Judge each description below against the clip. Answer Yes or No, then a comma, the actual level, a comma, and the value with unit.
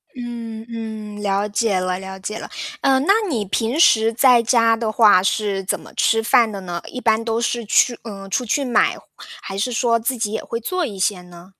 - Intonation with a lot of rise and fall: No, average, 2.9 semitones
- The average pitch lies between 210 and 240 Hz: Yes, high, 220 Hz